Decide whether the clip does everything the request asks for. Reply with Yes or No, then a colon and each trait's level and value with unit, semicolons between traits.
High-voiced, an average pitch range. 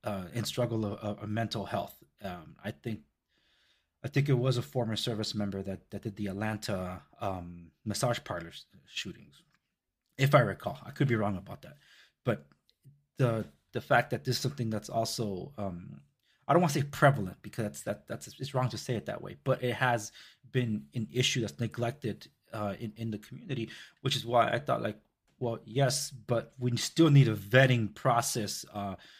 No: low, 115 Hz; average, 3.7 semitones